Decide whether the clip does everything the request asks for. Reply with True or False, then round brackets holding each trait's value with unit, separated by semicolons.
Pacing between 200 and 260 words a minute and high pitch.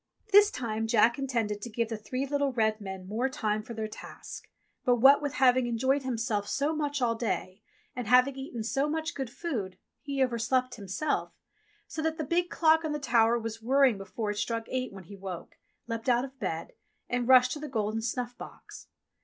True (205 wpm; 245 Hz)